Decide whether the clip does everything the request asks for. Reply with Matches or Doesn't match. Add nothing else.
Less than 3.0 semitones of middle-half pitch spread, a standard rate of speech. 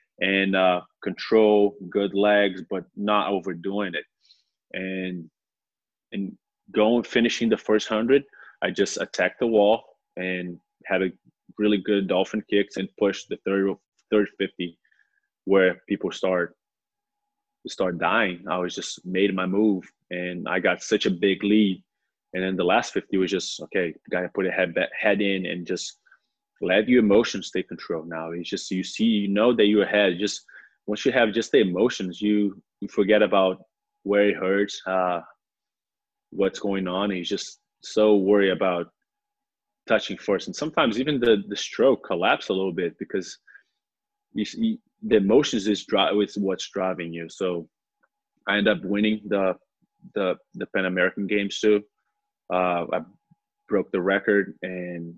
Matches